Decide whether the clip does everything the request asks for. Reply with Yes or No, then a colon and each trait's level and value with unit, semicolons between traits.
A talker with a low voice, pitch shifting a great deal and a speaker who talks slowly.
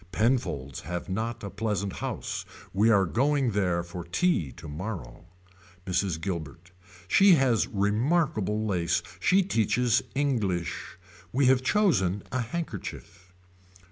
Yes: low, 100 Hz; wide, 6.1 semitones; slow, 115 wpm